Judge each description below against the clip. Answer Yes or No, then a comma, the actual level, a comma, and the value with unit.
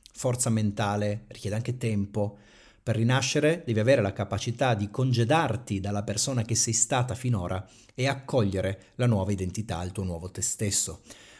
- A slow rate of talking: No, average, 155 wpm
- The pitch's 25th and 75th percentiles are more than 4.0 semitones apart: No, average, 3.4 semitones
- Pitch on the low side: Yes, low, 110 Hz